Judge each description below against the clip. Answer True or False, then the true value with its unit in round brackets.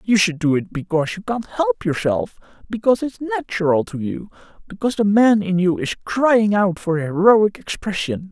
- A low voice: False (190 Hz)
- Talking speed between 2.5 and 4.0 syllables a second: False (4.9 syllables/s)